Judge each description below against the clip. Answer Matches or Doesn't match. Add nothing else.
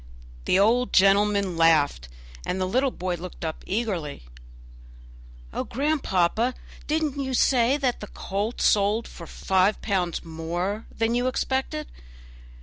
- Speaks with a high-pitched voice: Matches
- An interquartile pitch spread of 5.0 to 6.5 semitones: Matches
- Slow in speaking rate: Matches